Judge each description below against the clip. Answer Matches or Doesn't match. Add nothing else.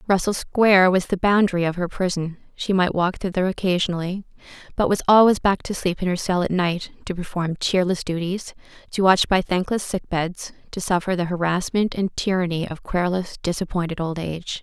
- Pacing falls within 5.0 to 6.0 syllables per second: Matches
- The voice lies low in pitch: Doesn't match